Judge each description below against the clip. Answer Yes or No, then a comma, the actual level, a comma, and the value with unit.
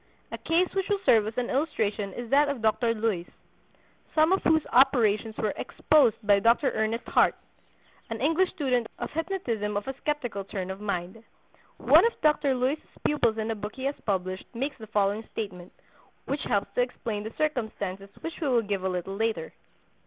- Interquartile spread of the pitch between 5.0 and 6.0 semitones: Yes, wide, 5.5 semitones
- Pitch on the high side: Yes, high, 225 Hz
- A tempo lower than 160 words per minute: No, average, 185 wpm